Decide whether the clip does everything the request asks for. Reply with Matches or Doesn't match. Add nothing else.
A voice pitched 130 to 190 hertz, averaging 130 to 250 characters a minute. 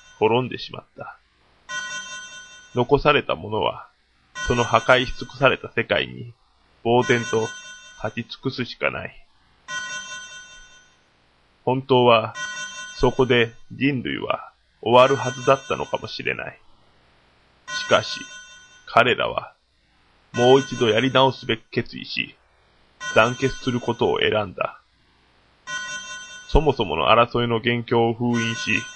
Matches